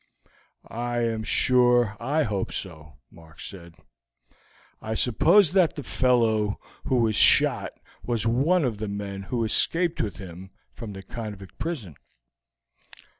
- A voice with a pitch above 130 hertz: No, low, 110 Hz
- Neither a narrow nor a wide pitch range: Yes, average, 4.3 semitones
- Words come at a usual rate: No, slow, 130 wpm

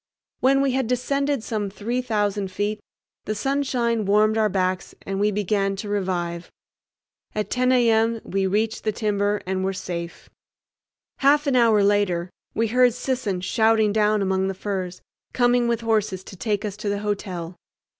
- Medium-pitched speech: No, high, 210 Hz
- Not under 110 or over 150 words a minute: No, average, 165 wpm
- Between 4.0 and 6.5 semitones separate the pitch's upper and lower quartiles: No, average, 3.3 semitones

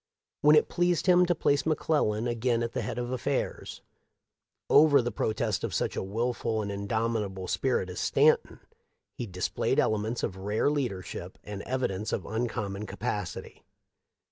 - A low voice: Yes, low, 115 Hz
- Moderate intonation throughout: Yes, average, 4.3 semitones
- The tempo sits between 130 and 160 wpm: Yes, average, 155 wpm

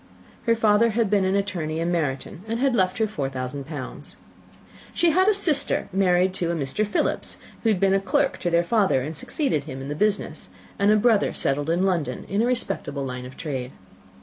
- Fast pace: Yes, fast, 210 wpm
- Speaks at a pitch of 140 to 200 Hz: Yes, medium, 185 Hz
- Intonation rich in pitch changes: Yes, wide, 6.5 semitones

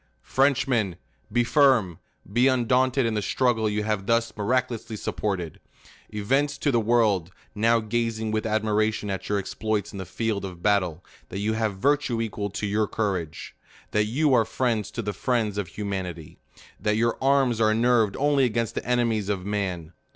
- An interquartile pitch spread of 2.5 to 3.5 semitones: Yes, average, 2.8 semitones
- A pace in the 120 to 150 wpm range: No, average, 175 wpm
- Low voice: Yes, low, 110 Hz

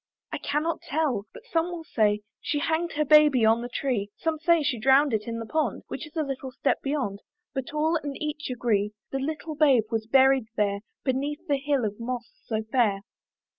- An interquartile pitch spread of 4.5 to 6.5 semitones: Yes, average, 4.9 semitones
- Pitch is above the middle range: Yes, very high, 270 Hz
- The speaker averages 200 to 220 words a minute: Yes, fast, 205 wpm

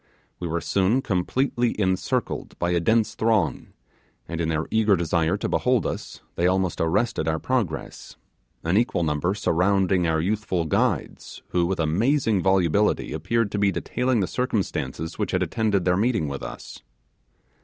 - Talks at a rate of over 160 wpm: No, average, 155 wpm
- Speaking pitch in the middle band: No, very low, 95 Hz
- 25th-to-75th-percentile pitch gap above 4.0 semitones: Yes, average, 4.5 semitones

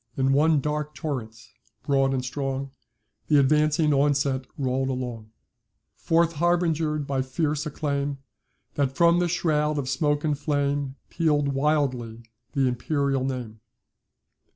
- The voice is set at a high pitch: No, medium, 140 Hz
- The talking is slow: Yes, slow, 125 wpm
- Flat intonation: Yes, narrow, 2.3 semitones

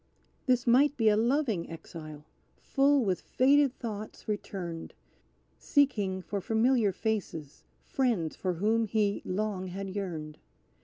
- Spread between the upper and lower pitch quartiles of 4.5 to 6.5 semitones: Yes, average, 4.8 semitones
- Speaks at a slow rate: Yes, slow, 120 wpm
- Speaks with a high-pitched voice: Yes, high, 210 Hz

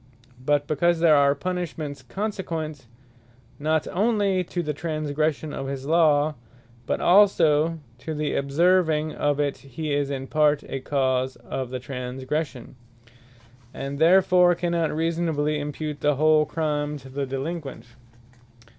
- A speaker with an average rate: No, slow, 130 wpm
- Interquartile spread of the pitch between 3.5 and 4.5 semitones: No, average, 2.8 semitones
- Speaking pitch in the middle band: Yes, medium, 150 Hz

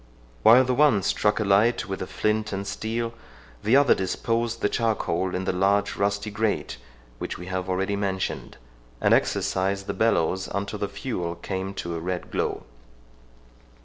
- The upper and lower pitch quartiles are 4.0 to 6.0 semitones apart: No, average, 2.8 semitones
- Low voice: Yes, low, 100 Hz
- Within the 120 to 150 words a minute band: No, average, 165 wpm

